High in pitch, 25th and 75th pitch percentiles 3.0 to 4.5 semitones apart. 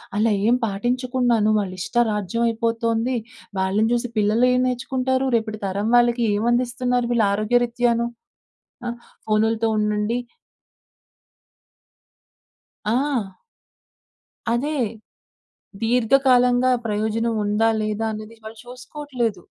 No: high, 230 Hz; narrow, 2.4 semitones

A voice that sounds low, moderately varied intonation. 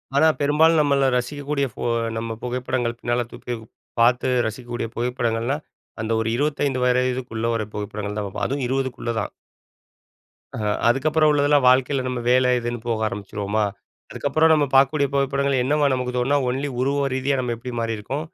Yes: low, 125 Hz; average, 3.1 semitones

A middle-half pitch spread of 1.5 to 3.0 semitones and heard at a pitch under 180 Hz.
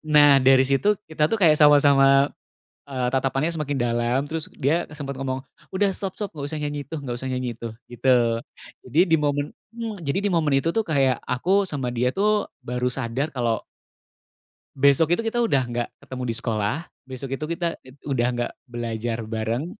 No: average, 4.0 semitones; medium, 140 Hz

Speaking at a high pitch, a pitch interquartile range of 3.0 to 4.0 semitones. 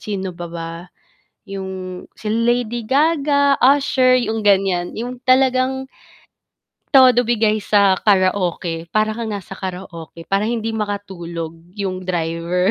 No: high, 205 Hz; average, 4.7 semitones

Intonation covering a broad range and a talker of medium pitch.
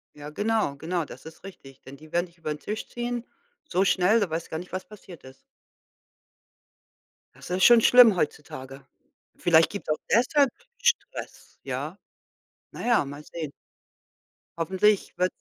Yes: wide, 5.7 semitones; medium, 180 Hz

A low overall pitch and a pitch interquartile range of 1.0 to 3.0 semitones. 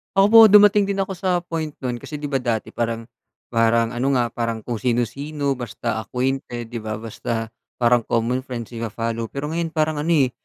No: low, 125 Hz; average, 4.7 semitones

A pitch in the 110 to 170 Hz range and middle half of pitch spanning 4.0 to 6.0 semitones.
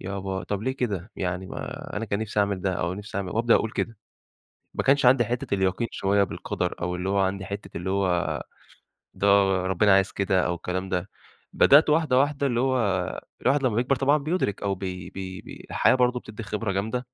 No: low, 100 Hz; average, 4.6 semitones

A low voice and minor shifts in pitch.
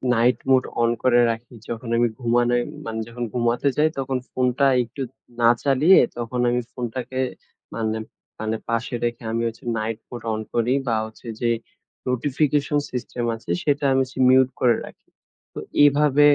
Yes: low, 120 Hz; narrow, 2.1 semitones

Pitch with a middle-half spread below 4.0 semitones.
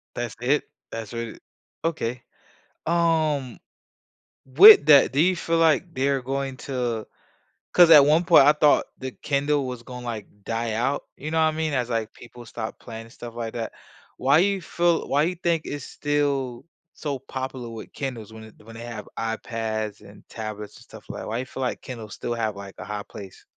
No: average, 4.6 semitones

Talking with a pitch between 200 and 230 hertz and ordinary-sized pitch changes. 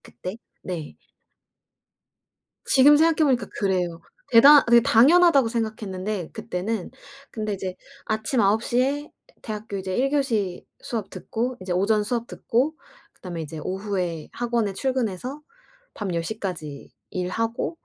Yes: high, 220 Hz; average, 5.0 semitones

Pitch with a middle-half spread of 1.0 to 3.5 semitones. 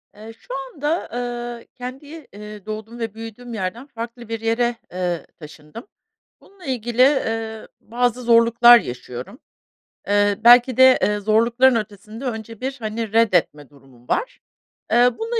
Yes: average, 2.8 semitones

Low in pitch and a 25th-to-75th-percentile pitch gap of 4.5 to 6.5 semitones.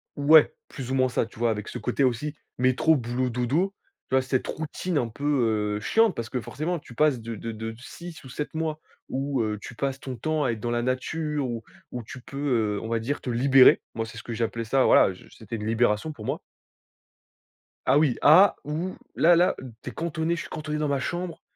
Yes: low, 130 Hz; average, 4.8 semitones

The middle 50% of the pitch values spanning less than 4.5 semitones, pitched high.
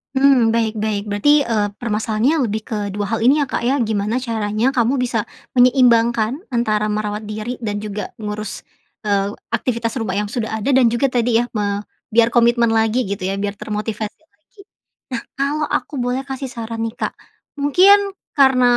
Yes: average, 3.0 semitones; high, 225 Hz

